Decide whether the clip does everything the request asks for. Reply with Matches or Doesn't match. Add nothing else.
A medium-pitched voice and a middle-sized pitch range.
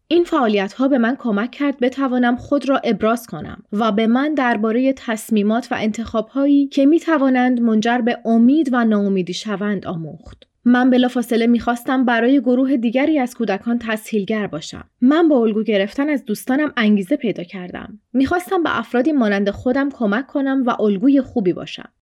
Doesn't match